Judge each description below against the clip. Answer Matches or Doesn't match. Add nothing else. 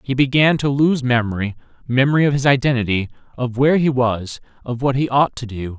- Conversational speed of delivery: Matches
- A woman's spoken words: Doesn't match